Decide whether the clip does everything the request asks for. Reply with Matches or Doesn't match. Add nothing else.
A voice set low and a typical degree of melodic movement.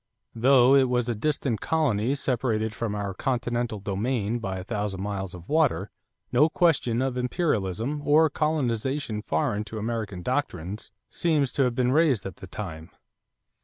Matches